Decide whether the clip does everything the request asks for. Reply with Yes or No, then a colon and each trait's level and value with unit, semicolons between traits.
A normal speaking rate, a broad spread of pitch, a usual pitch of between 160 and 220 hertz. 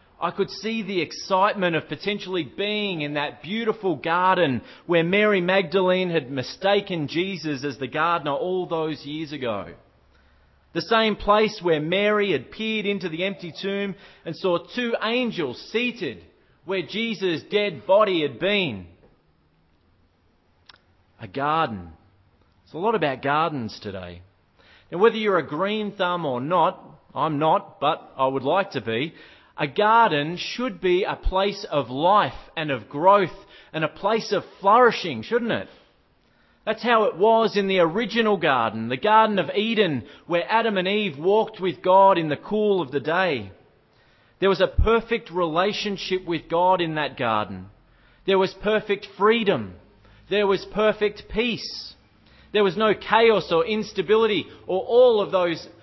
Yes: average, 155 wpm; wide, 6.2 semitones; medium, 185 Hz